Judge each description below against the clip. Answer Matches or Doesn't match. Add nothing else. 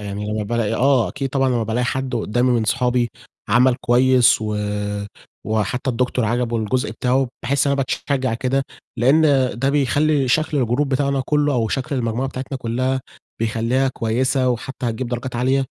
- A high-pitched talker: Doesn't match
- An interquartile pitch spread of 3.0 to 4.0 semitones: Doesn't match